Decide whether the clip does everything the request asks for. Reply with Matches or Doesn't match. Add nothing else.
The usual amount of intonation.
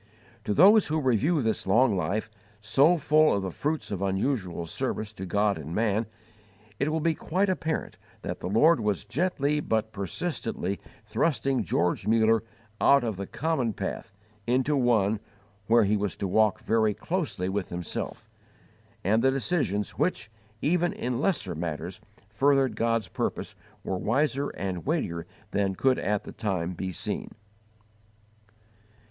Doesn't match